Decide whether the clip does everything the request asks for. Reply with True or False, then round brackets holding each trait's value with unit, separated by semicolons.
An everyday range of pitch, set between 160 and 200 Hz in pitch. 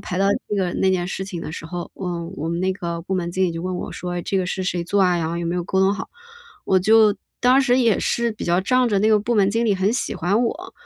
True (3.4 semitones; 190 Hz)